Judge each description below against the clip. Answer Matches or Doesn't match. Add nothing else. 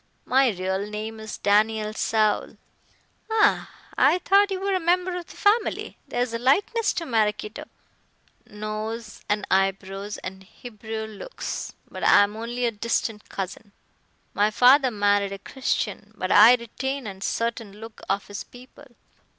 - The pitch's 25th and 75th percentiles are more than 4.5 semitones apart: Doesn't match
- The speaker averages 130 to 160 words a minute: Matches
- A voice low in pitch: Doesn't match